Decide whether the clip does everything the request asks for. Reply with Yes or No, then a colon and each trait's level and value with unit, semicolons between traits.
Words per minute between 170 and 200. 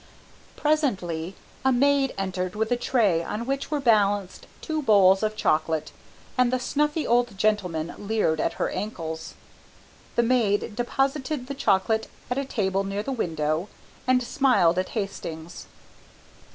No: average, 140 wpm